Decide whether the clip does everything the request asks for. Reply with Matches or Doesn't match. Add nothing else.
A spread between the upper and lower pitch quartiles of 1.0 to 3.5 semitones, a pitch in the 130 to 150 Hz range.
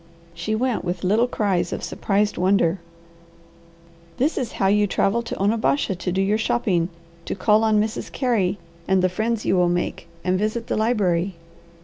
Doesn't match